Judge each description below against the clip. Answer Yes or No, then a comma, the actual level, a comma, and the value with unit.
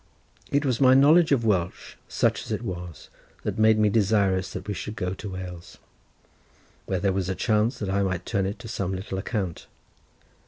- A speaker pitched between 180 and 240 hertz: No, low, 100 Hz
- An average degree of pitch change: Yes, average, 3.0 semitones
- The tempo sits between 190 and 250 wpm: Yes, average, 195 wpm